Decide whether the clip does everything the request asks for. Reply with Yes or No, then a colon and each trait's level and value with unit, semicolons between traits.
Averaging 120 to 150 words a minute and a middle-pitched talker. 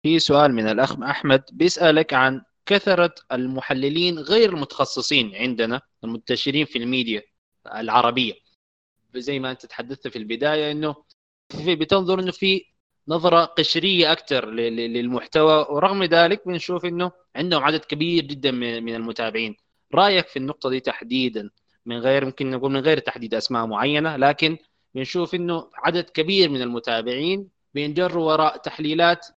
Yes: fast, 135 wpm; medium, 145 Hz